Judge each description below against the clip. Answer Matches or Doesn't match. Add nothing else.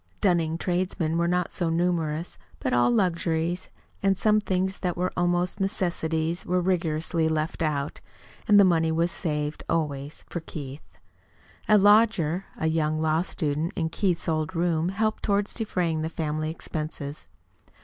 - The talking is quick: Doesn't match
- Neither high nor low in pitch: Matches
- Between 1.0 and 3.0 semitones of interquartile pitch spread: Matches